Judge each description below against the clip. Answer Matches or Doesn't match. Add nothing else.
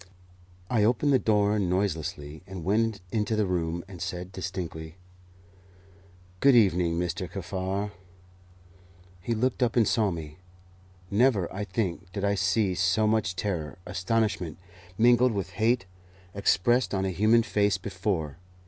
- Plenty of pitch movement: Doesn't match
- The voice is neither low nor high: Doesn't match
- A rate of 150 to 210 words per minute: Doesn't match